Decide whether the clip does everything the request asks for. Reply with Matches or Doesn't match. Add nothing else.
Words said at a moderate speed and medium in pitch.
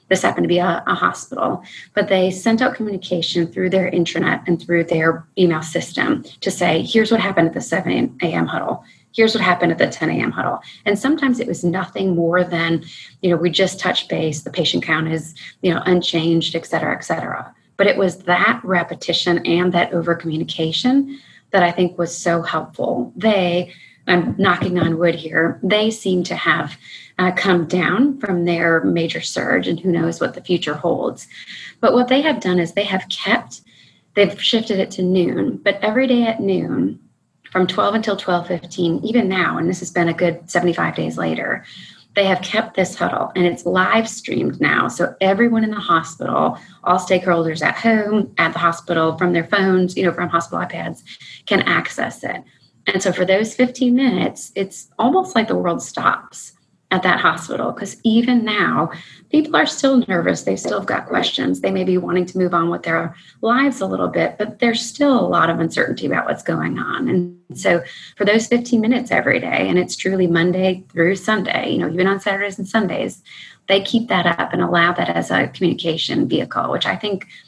Matches